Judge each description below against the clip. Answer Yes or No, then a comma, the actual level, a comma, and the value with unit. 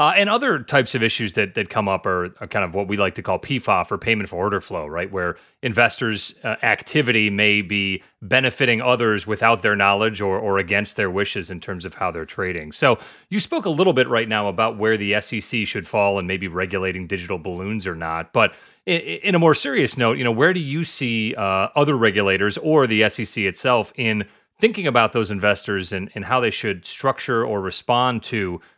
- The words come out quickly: Yes, fast, 215 wpm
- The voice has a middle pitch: No, low, 110 Hz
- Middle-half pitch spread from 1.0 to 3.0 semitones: No, average, 4.0 semitones